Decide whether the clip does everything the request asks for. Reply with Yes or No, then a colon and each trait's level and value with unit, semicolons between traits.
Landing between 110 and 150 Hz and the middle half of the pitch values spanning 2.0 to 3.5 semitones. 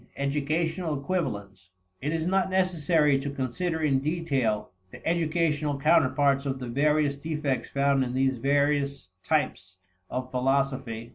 Yes: medium, 140 Hz; average, 3.1 semitones